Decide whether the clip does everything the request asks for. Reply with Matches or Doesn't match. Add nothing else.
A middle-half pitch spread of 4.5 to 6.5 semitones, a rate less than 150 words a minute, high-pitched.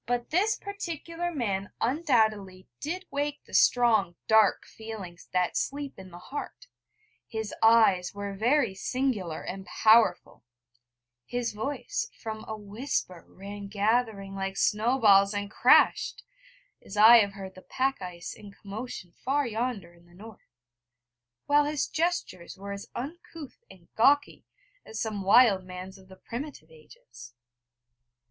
Matches